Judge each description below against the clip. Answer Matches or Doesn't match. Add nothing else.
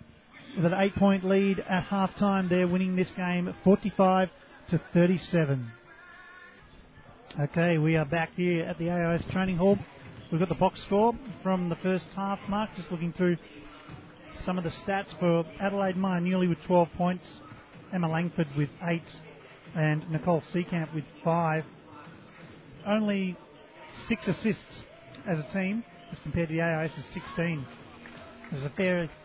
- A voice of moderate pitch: Matches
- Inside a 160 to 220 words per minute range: Doesn't match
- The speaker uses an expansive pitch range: Doesn't match